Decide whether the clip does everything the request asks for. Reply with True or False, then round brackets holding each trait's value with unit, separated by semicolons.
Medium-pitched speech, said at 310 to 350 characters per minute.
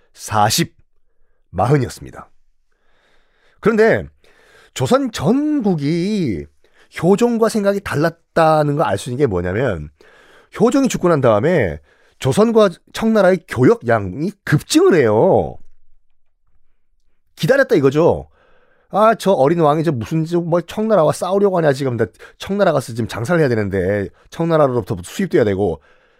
False (175 Hz; 260 characters per minute)